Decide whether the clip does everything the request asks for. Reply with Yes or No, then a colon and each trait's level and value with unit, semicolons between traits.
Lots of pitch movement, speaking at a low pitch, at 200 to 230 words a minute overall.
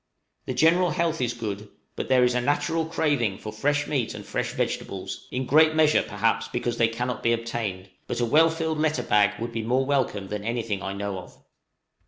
Yes: wide, 5.7 semitones; low, 120 Hz; fast, 205 wpm